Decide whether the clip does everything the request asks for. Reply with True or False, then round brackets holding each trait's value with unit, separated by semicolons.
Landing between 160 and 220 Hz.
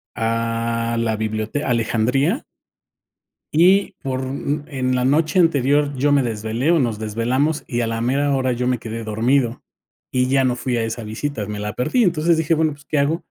False (130 Hz)